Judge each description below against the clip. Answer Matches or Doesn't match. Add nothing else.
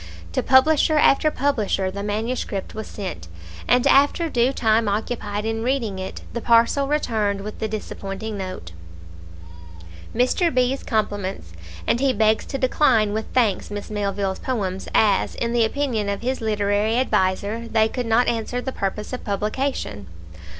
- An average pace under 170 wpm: Matches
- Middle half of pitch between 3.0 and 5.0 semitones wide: Matches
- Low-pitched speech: Doesn't match